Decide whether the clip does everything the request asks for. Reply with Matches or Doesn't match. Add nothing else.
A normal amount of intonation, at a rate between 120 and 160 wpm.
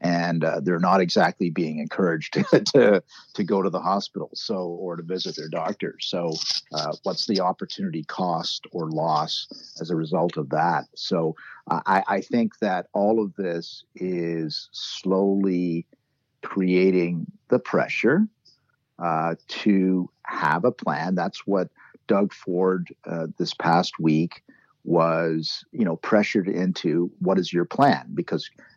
Doesn't match